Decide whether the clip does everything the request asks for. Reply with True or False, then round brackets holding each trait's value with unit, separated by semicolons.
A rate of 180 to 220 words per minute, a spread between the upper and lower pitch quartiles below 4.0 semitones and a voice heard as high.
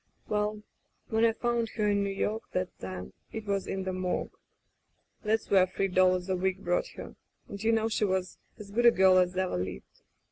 True (205 wpm; 2.9 semitones; 195 Hz)